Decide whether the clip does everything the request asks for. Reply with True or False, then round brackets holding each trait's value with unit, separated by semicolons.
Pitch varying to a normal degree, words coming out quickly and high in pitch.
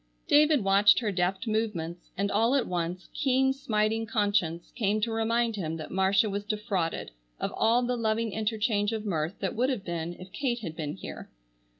False (3.5 semitones; 185 wpm; 210 Hz)